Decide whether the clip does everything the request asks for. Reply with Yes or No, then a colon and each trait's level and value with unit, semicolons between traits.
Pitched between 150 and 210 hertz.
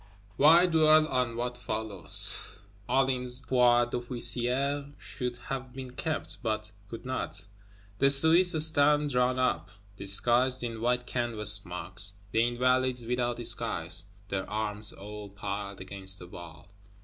No: low, 120 Hz